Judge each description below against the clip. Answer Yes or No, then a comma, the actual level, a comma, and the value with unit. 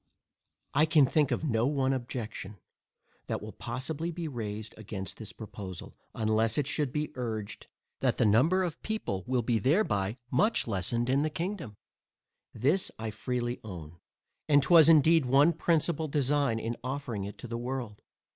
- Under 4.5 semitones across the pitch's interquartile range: No, wide, 5.4 semitones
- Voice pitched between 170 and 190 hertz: No, low, 125 Hz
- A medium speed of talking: Yes, average, 160 wpm